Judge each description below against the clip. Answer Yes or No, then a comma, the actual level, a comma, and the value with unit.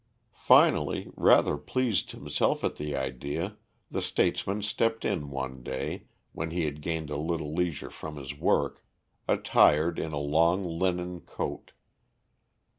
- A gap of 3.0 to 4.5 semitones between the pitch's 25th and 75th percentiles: Yes, average, 3.4 semitones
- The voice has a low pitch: Yes, very low, 80 Hz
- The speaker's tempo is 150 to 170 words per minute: No, slow, 135 wpm